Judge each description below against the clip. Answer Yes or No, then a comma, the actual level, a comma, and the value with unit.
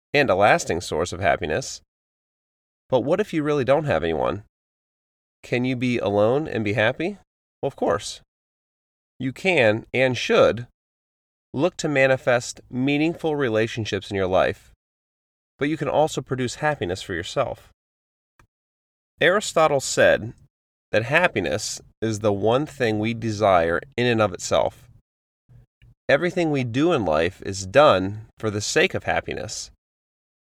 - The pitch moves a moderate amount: No, wide, 6.2 semitones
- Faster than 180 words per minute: No, average, 140 wpm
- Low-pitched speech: Yes, low, 115 Hz